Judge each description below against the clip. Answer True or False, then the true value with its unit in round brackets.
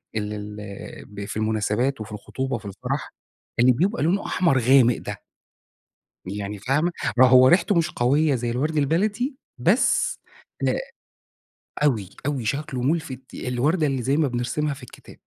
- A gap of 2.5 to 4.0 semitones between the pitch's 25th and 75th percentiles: False (5.5 semitones)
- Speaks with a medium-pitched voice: False (130 Hz)